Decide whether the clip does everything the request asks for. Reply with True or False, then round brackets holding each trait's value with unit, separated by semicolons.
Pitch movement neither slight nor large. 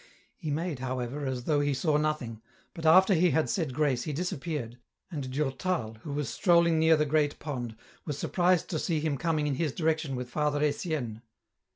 True (3.5 semitones)